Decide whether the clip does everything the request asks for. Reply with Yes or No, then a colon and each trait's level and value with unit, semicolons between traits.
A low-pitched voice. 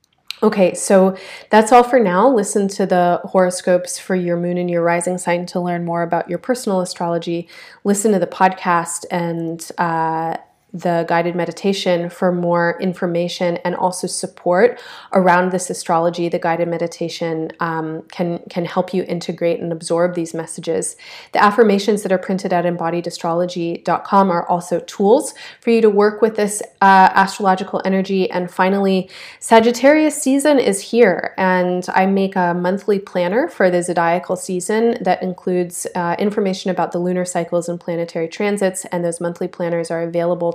No: medium, 180 Hz